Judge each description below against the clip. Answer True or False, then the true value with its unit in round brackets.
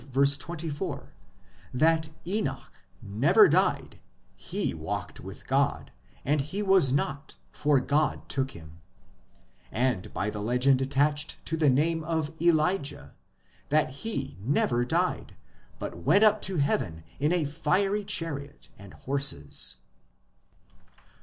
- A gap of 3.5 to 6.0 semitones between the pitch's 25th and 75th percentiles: True (4.0 semitones)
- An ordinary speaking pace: False (125 wpm)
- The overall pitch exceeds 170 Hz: False (145 Hz)